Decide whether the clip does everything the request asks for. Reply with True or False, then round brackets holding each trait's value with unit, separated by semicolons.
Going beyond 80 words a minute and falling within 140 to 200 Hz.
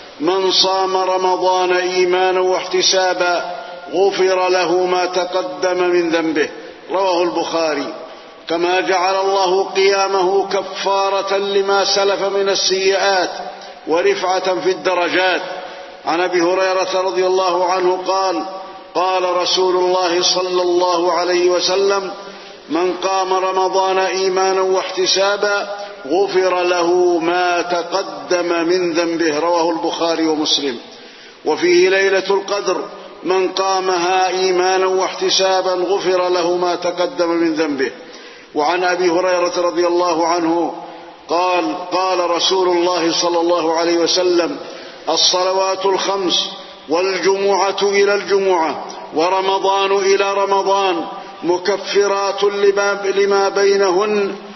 True (100 wpm; 185 Hz)